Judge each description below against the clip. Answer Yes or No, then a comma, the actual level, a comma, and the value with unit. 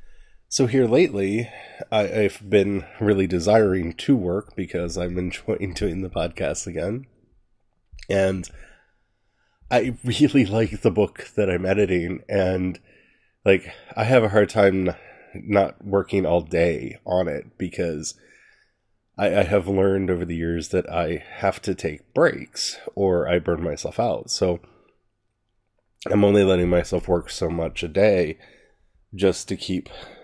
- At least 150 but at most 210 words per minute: No, average, 140 wpm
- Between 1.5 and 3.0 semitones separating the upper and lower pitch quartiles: Yes, average, 2.7 semitones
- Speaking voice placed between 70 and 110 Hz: Yes, very low, 95 Hz